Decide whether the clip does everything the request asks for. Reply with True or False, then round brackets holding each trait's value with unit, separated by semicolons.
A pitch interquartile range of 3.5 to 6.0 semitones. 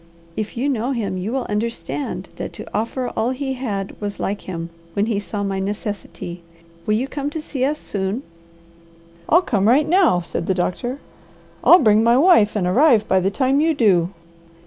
True (5.2 semitones)